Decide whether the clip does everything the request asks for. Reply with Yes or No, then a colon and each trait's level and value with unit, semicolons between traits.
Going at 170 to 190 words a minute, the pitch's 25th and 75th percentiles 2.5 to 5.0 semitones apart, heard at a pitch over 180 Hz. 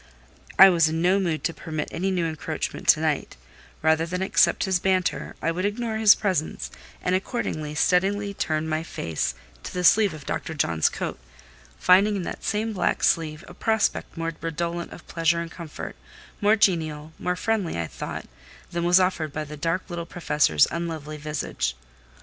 No: average, 175 wpm; average, 3.3 semitones; medium, 170 Hz